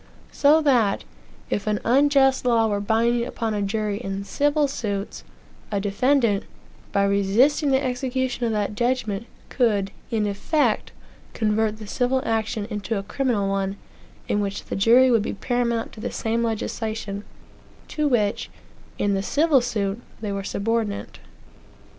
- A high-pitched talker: Yes, high, 225 Hz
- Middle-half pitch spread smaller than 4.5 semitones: Yes, average, 3.7 semitones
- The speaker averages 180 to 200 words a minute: No, average, 145 wpm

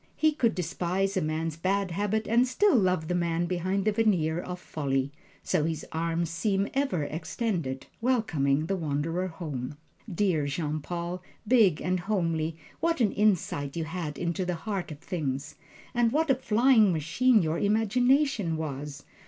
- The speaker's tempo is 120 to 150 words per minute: No, average, 160 wpm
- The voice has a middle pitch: Yes, medium, 175 Hz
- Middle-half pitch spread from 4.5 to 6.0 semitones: Yes, average, 5.0 semitones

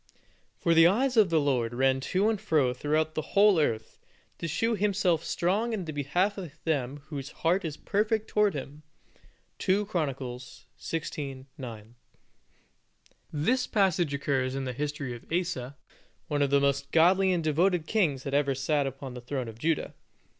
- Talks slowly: No, average, 170 wpm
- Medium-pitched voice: Yes, medium, 155 Hz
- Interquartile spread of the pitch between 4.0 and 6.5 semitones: Yes, average, 5.3 semitones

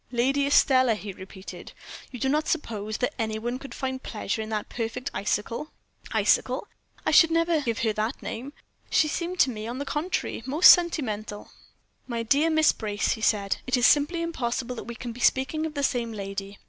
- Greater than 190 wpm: Yes, average, 200 wpm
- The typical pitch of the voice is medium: No, high, 245 Hz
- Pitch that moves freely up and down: No, average, 4.8 semitones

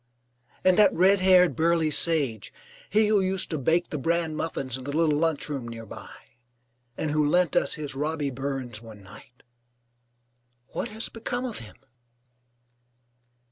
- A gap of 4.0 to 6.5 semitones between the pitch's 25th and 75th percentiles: Yes, average, 5.0 semitones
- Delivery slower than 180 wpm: Yes, average, 150 wpm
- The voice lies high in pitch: No, medium, 155 Hz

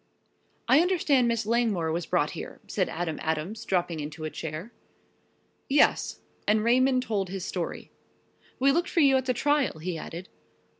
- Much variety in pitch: Yes, wide, 7.6 semitones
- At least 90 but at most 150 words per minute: No, average, 160 wpm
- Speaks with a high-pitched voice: Yes, high, 215 Hz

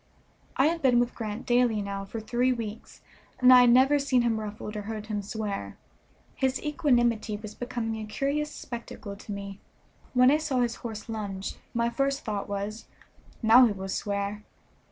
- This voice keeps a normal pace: Yes, average, 175 wpm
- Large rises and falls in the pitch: No, average, 3.3 semitones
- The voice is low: No, high, 225 Hz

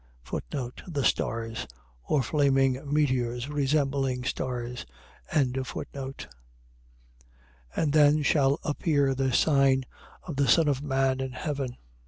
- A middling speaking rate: No, slow, 105 wpm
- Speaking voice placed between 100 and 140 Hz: Yes, low, 135 Hz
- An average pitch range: No, narrow, 2.0 semitones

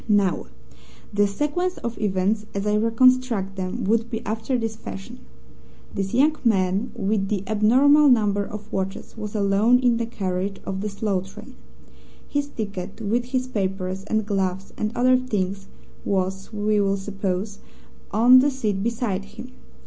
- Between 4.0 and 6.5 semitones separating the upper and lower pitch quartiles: No, average, 3.2 semitones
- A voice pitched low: No, high, 210 Hz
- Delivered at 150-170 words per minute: Yes, average, 155 wpm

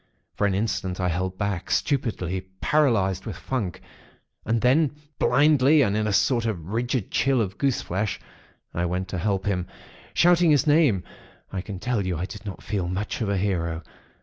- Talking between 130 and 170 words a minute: No, average, 180 wpm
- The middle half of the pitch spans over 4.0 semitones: Yes, average, 5.1 semitones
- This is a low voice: Yes, low, 100 Hz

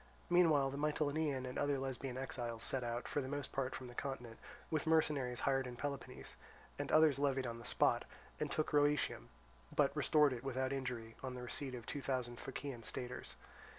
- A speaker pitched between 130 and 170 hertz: Yes, low, 135 Hz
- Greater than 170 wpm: Yes, average, 185 wpm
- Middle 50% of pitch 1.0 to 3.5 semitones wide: Yes, narrow, 2.6 semitones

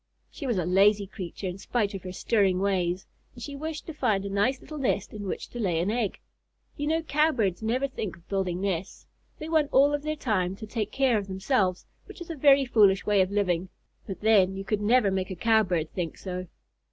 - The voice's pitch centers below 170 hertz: No, high, 205 Hz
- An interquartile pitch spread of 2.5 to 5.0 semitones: No, wide, 5.4 semitones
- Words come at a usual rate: No, fast, 225 wpm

